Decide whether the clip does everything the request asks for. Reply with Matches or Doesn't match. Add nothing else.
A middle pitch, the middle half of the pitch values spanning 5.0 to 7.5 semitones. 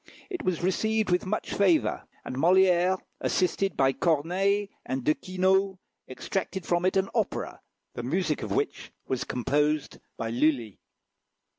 Matches